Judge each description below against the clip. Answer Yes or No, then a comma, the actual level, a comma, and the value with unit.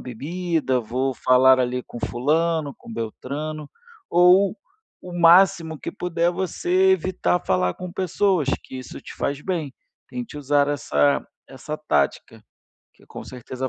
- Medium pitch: Yes, medium, 150 Hz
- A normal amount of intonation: No, wide, 5.7 semitones